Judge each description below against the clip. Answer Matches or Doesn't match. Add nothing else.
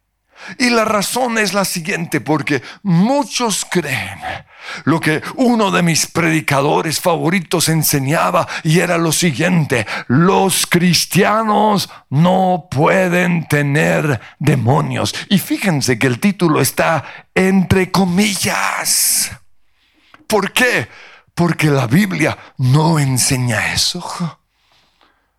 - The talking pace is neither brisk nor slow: Doesn't match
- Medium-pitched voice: Matches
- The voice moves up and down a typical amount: Matches